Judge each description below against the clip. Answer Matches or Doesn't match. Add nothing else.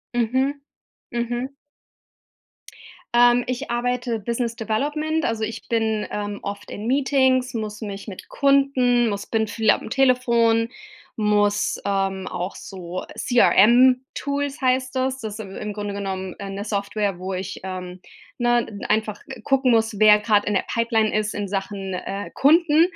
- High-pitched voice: Matches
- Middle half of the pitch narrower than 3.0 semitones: Doesn't match